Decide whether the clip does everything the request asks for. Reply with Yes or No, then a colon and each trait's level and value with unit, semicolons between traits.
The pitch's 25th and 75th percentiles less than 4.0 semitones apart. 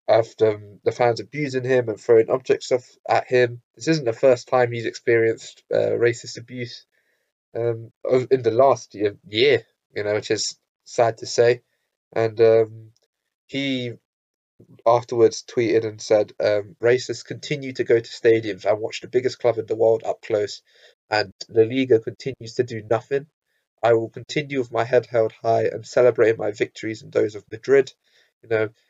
No: average, 4.4 semitones